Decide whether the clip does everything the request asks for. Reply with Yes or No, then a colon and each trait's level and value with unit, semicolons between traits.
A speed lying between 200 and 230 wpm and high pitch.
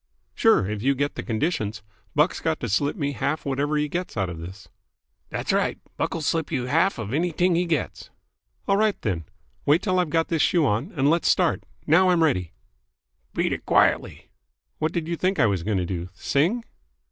No: fast, 205 wpm; medium, 145 Hz